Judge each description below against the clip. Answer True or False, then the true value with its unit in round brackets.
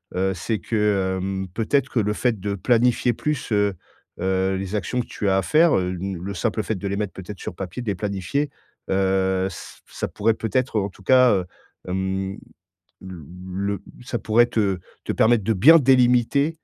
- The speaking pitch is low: True (100 Hz)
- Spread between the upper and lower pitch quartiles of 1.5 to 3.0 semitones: False (4.0 semitones)